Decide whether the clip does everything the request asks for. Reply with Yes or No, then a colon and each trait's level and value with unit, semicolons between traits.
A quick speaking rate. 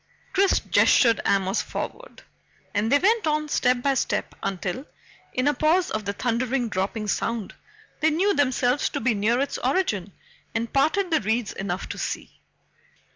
No: average, 160 wpm